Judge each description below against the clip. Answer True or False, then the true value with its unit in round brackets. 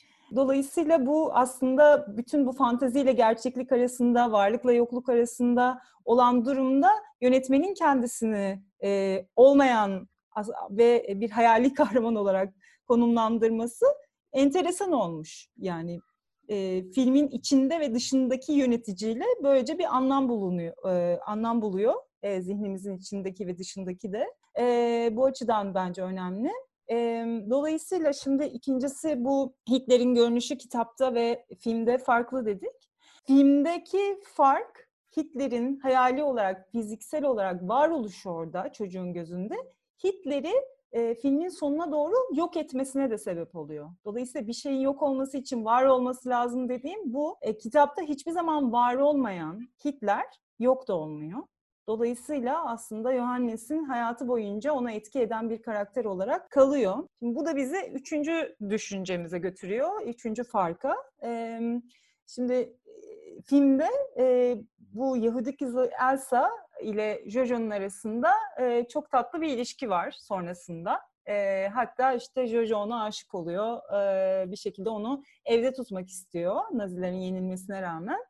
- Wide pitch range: False (4.5 semitones)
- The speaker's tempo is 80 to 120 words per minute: True (115 wpm)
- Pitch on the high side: True (245 Hz)